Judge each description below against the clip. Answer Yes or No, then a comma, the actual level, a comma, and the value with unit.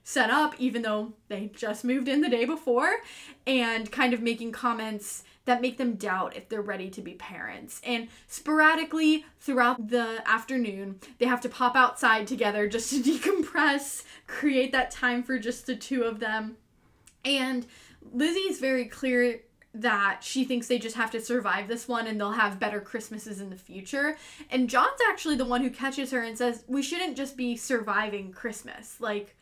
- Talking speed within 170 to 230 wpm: Yes, average, 180 wpm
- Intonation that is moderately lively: Yes, average, 3.1 semitones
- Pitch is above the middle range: Yes, high, 245 Hz